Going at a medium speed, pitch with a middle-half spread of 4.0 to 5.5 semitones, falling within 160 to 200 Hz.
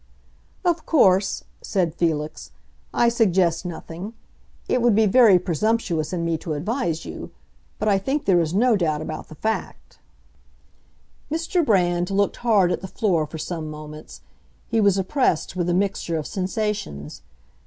Yes: average, 155 wpm; average, 4.9 semitones; medium, 185 Hz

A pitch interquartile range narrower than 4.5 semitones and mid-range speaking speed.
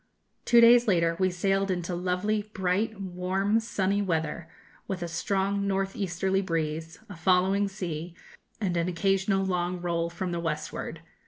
Yes: narrow, 2.4 semitones; average, 150 wpm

